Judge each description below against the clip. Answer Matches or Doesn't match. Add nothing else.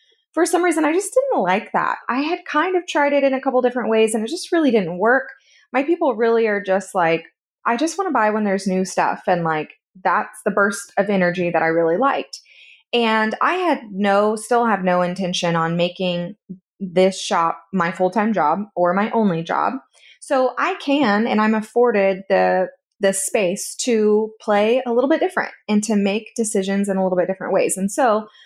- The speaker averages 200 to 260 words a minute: Matches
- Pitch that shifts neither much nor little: Doesn't match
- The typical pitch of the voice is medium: Doesn't match